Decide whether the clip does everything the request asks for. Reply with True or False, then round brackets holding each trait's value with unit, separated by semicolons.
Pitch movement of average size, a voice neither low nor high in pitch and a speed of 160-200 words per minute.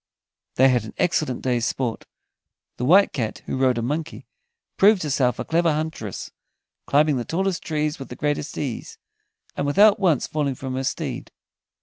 True (4.2 semitones; 145 Hz; 165 wpm)